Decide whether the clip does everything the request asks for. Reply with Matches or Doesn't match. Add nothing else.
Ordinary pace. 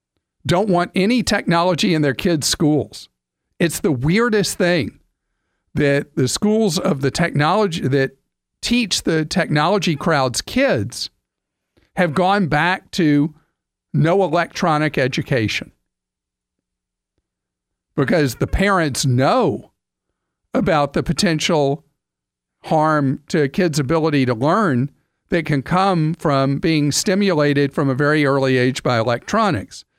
Doesn't match